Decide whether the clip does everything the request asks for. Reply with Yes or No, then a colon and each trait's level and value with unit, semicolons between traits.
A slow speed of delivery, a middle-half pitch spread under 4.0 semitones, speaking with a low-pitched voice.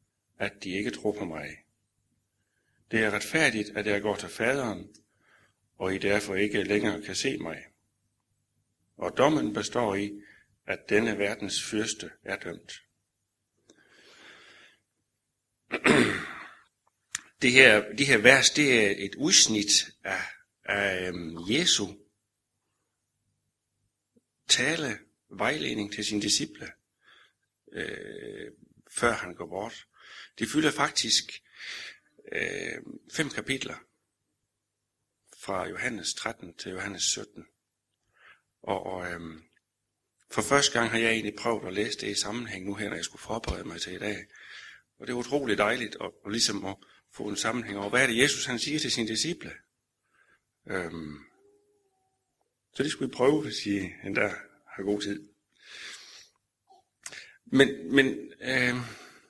Yes: slow, 130 wpm; average, 3.3 semitones; low, 105 Hz